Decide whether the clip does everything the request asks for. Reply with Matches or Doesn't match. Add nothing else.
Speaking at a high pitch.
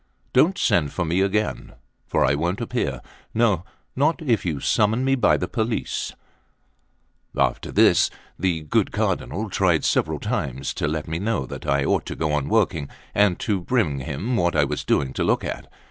Doesn't match